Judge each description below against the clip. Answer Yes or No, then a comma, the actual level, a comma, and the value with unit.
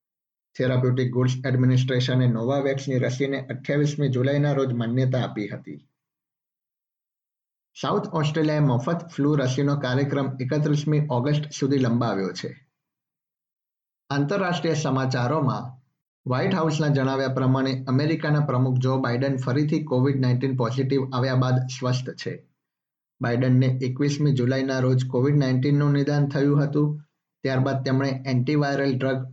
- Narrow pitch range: Yes, narrow, 2.1 semitones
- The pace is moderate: No, slow, 65 wpm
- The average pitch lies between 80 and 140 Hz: Yes, low, 135 Hz